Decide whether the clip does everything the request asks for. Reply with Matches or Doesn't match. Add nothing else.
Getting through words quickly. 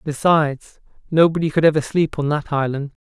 Doesn't match